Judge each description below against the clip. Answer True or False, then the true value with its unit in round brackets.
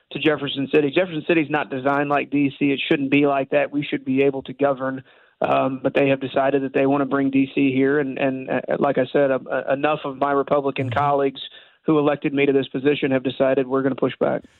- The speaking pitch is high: False (140 Hz)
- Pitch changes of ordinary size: False (1.1 semitones)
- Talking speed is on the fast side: True (240 wpm)